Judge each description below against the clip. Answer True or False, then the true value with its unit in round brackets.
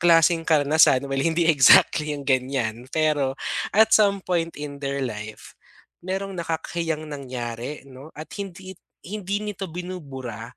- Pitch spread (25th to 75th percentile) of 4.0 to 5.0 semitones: True (4.7 semitones)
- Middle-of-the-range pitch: True (155 Hz)